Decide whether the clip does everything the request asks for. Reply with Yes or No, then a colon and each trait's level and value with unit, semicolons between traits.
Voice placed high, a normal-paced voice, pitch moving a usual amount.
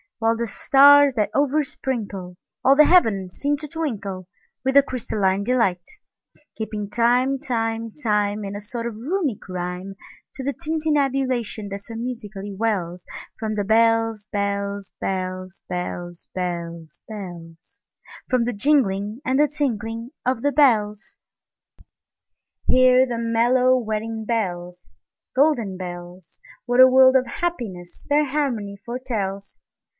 No: high, 225 Hz; slow, 110 wpm; average, 4.8 semitones